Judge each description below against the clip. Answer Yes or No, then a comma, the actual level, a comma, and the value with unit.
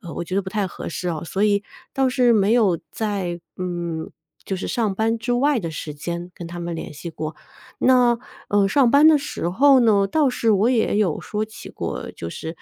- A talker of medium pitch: No, high, 200 Hz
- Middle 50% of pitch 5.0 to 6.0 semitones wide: Yes, wide, 5.5 semitones